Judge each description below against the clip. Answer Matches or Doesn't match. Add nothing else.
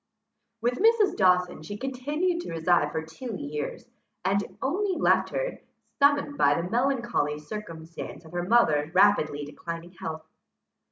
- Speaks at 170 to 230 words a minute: Doesn't match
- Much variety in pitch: Matches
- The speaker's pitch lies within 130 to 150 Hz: Doesn't match